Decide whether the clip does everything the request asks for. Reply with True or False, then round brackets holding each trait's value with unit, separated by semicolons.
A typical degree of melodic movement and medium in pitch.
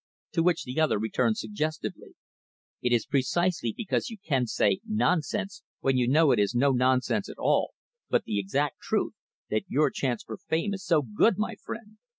False (7.6 semitones; 150 Hz)